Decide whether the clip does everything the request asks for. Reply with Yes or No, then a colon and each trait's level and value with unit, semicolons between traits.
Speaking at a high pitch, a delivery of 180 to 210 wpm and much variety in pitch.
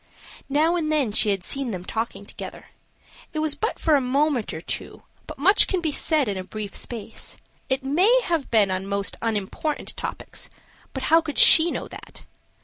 Yes: very high, 270 Hz; average, 190 wpm; wide, 7.1 semitones